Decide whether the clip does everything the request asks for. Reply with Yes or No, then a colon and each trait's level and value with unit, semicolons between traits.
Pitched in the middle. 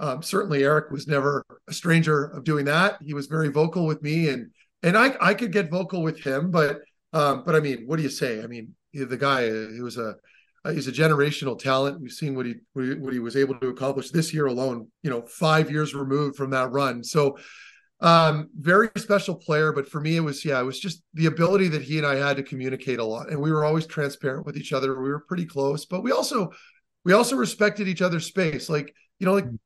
Yes: medium, 150 Hz